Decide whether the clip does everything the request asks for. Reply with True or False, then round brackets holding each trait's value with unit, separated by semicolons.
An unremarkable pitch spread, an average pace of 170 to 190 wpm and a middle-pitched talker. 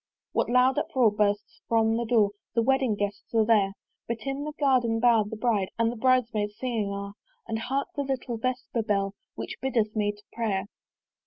False (3.3 semitones; 185 wpm; 225 Hz)